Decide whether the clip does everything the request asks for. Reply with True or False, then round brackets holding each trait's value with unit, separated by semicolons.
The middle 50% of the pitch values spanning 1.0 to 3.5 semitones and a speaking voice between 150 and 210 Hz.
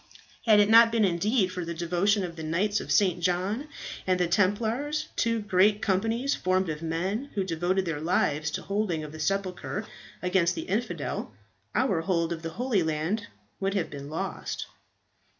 False (3.9 semitones; 185 Hz)